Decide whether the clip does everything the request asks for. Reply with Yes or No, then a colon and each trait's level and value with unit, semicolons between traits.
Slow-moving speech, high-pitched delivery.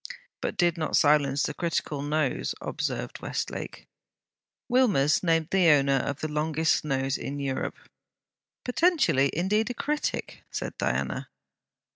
No: slow, 125 wpm; medium, 155 Hz